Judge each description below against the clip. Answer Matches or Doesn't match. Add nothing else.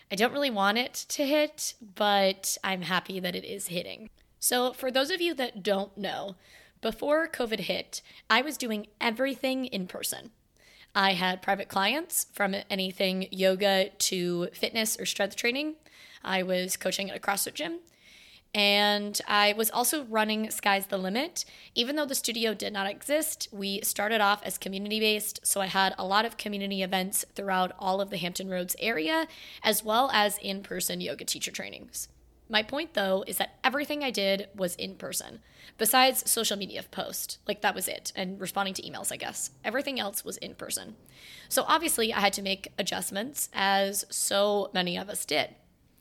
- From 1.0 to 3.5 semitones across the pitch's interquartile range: Doesn't match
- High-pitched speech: Matches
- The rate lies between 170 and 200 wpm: Matches